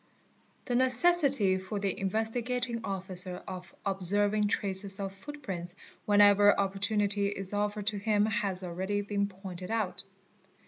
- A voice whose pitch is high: Yes, high, 200 Hz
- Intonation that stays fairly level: Yes, narrow, 2.1 semitones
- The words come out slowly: Yes, slow, 130 wpm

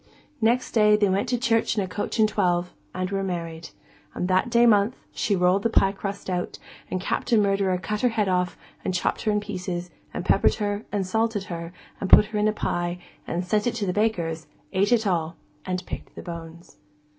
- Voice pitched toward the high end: Yes, high, 195 Hz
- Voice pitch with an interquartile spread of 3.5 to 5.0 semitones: No, average, 2.9 semitones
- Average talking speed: No, fast, 215 wpm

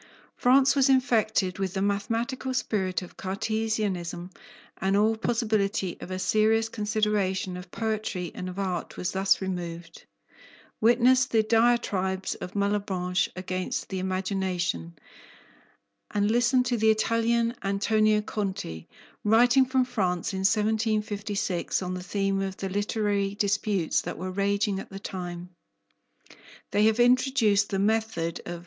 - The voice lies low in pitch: No, high, 200 Hz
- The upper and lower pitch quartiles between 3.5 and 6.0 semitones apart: No, average, 2.9 semitones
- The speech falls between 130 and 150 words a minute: Yes, slow, 135 wpm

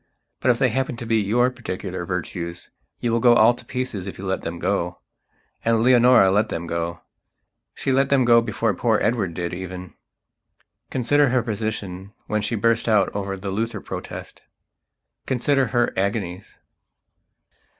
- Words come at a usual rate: Yes, average, 160 wpm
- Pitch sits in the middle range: No, low, 110 Hz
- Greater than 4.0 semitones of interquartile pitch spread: Yes, average, 4.4 semitones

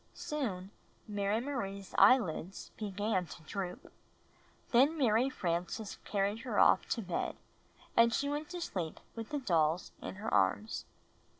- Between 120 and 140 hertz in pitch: No, high, 210 Hz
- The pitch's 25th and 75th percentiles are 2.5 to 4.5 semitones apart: No, average, 5.3 semitones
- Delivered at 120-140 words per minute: Yes, slow, 135 wpm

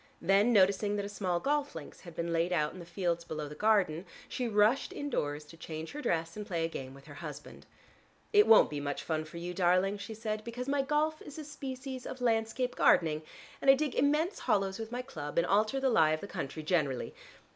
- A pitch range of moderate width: No, wide, 7.3 semitones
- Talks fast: Yes, fast, 225 wpm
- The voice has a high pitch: Yes, high, 195 Hz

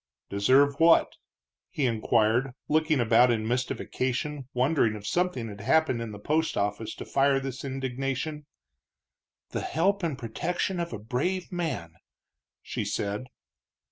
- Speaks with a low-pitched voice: Yes, low, 130 Hz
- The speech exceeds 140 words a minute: No, slow, 135 wpm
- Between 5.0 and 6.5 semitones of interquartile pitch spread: Yes, wide, 5.5 semitones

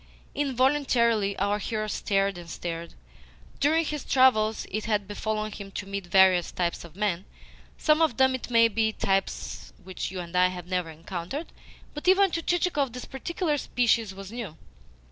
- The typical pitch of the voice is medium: No, high, 215 Hz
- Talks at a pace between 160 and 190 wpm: Yes, average, 165 wpm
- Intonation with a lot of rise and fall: Yes, wide, 5.9 semitones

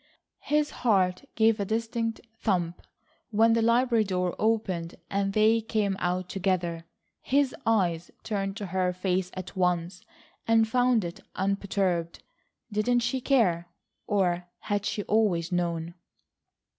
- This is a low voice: No, high, 195 Hz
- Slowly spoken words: Yes, slow, 130 wpm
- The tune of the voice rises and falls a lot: No, average, 3.9 semitones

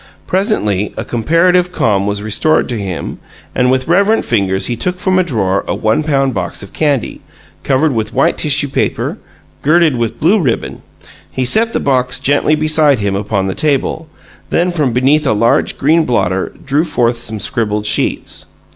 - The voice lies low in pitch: Yes, low, 130 Hz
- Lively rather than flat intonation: Yes, wide, 6.3 semitones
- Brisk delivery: No, average, 175 wpm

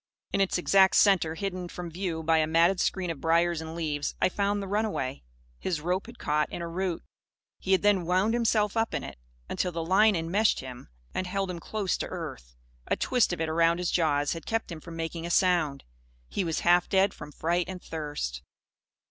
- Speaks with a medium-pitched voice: Yes, medium, 175 Hz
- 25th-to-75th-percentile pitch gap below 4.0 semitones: Yes, average, 3.0 semitones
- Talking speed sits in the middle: No, fast, 210 wpm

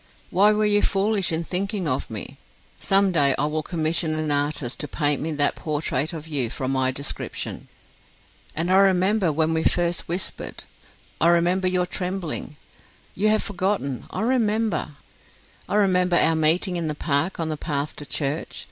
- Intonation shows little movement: No, average, 4.2 semitones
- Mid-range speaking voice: Yes, medium, 165 Hz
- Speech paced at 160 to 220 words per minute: Yes, average, 170 wpm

